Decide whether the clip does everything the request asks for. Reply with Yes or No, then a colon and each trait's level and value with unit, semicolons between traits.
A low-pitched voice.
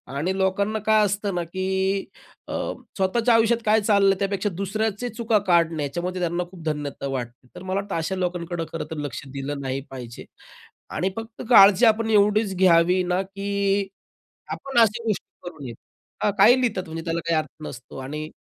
No: high, 190 Hz